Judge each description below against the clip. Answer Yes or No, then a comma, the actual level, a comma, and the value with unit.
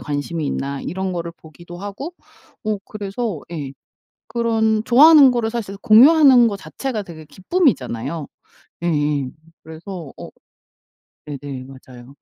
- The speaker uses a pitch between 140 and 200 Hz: Yes, medium, 185 Hz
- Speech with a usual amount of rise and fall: No, wide, 7.7 semitones